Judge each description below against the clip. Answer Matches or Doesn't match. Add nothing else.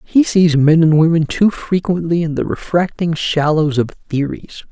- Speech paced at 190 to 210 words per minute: Doesn't match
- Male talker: Matches